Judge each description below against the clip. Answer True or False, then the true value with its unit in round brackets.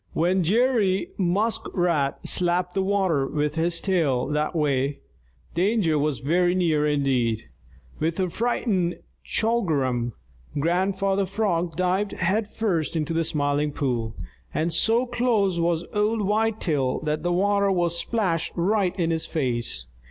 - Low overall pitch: False (175 Hz)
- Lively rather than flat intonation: False (4.7 semitones)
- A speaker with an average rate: False (130 wpm)